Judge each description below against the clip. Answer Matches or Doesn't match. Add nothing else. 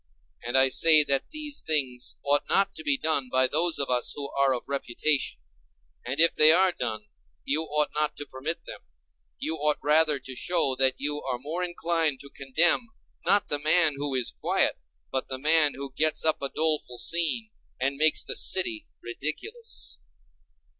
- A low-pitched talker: Doesn't match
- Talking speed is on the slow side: Doesn't match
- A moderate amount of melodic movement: Matches